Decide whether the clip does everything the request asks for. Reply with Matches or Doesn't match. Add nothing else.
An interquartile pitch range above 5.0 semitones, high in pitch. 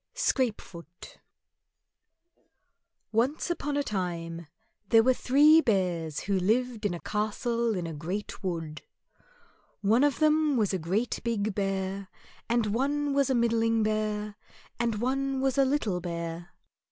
Matches